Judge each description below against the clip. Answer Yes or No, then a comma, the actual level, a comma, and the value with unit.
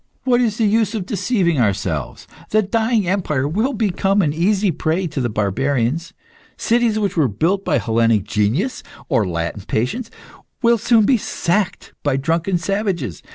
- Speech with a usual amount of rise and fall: No, wide, 8.8 semitones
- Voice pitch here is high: No, medium, 175 Hz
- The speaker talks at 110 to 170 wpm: Yes, average, 155 wpm